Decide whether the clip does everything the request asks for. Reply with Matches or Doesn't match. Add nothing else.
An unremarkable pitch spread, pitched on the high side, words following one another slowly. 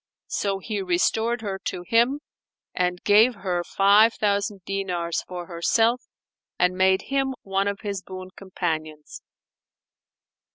Matches